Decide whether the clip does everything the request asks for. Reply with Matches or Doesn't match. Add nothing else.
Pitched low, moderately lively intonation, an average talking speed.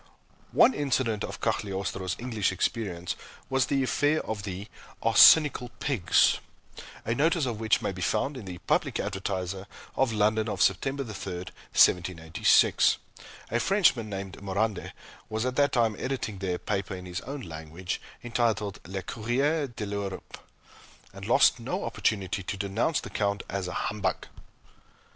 Matches